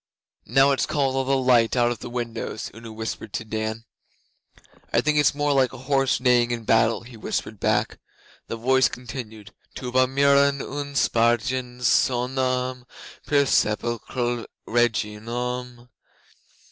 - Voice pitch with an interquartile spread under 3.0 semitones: Yes, narrow, 2.4 semitones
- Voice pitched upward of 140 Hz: No, low, 125 Hz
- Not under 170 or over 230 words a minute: No, slow, 135 wpm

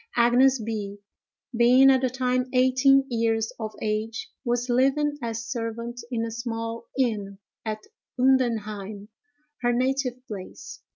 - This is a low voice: No, high, 240 Hz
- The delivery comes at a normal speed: No, slow, 125 wpm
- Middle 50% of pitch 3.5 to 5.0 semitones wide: No, narrow, 2.5 semitones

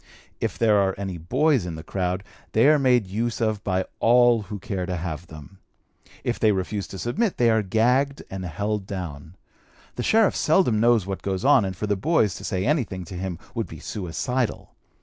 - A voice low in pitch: Yes, low, 105 Hz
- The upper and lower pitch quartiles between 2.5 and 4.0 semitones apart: No, average, 4.6 semitones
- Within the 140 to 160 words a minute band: No, average, 200 wpm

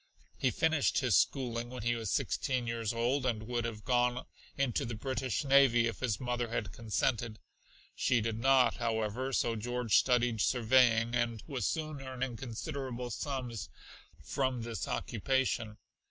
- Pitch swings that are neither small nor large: No, narrow, 2.3 semitones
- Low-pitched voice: Yes, low, 120 Hz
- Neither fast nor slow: Yes, average, 150 wpm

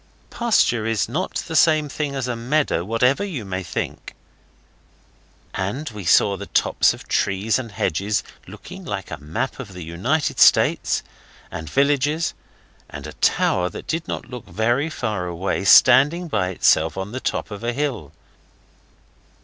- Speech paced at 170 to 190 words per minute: No, average, 160 wpm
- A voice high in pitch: No, low, 115 Hz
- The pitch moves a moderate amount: No, wide, 7.3 semitones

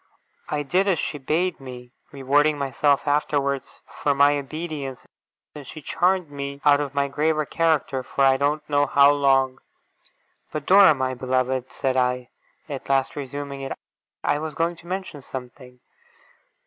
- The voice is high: No, medium, 140 Hz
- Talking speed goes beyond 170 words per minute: No, average, 155 wpm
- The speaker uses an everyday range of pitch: No, narrow, 2.2 semitones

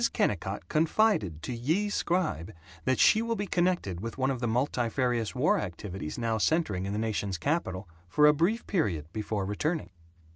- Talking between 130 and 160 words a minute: No, average, 170 wpm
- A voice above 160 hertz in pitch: No, low, 120 Hz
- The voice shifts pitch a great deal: Yes, wide, 8.5 semitones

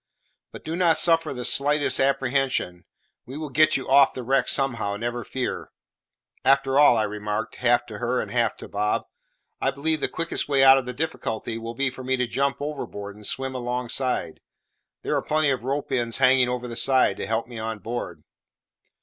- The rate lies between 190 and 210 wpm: Yes, average, 195 wpm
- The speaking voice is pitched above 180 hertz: No, low, 130 Hz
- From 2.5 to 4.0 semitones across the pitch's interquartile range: Yes, average, 2.8 semitones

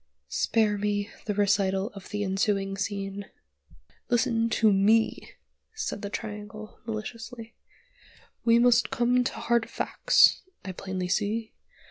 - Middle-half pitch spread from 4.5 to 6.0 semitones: No, narrow, 2.5 semitones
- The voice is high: Yes, high, 210 Hz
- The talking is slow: Yes, slow, 120 wpm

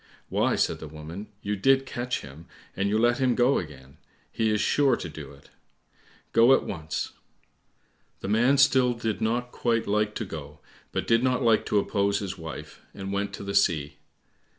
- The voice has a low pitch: Yes, low, 105 Hz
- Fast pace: No, average, 185 wpm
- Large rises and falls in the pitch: Yes, wide, 6.1 semitones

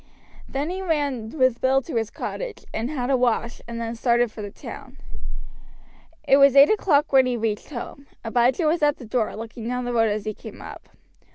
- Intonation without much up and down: No, average, 3.7 semitones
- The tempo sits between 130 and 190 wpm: No, fast, 205 wpm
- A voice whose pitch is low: No, very high, 250 Hz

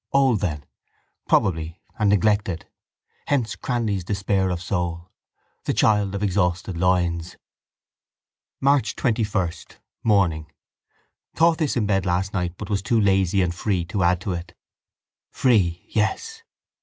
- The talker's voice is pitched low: Yes, very low, 95 Hz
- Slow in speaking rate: Yes, slow, 130 wpm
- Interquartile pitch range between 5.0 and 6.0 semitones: No, average, 3.4 semitones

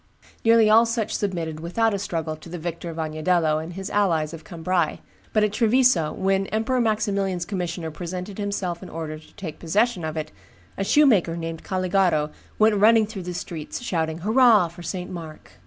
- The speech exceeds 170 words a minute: Yes, average, 180 wpm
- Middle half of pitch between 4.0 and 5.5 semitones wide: Yes, average, 4.4 semitones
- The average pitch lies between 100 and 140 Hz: No, medium, 180 Hz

